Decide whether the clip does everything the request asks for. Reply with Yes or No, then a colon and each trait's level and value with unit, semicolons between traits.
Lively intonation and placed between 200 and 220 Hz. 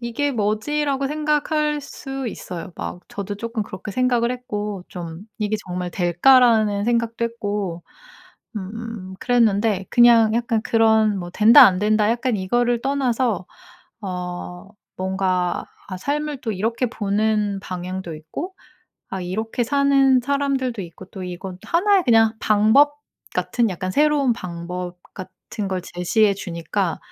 No: average, 4.9 semitones; high, 215 Hz